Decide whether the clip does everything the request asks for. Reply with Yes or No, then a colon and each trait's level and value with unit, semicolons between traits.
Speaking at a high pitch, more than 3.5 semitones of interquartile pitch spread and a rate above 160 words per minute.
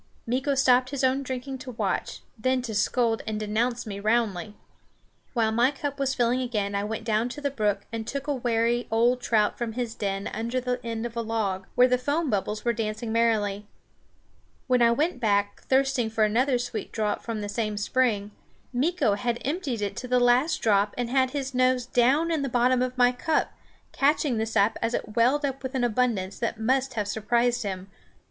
No: high, 240 Hz; average, 2.9 semitones; average, 200 wpm